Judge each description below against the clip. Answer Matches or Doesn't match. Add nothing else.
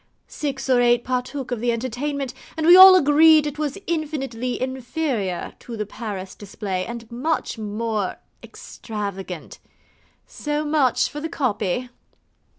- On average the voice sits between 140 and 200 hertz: Doesn't match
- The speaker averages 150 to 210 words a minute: Doesn't match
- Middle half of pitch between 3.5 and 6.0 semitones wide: Matches